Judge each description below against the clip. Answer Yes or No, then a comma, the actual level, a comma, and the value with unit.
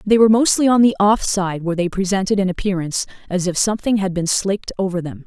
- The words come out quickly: Yes, fast, 230 wpm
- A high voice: Yes, high, 195 Hz